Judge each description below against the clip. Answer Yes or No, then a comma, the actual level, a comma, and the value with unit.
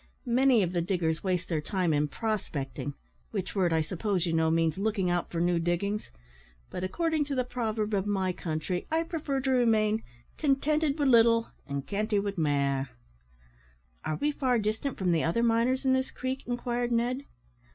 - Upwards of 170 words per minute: Yes, average, 180 wpm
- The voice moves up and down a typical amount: No, wide, 6.4 semitones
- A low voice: No, high, 210 Hz